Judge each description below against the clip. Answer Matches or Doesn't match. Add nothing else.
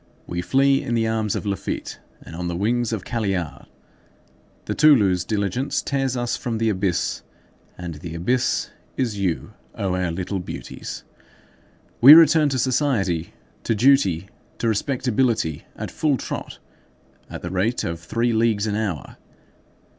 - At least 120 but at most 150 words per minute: Matches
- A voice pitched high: Doesn't match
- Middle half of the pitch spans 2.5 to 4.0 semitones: Doesn't match